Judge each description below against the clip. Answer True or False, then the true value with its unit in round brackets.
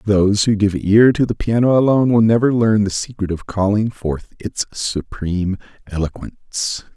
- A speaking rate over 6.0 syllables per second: False (4.9 syllables/s)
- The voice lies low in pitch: True (105 Hz)